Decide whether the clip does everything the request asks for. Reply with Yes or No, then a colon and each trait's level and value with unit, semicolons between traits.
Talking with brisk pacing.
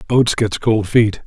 No: average, 190 wpm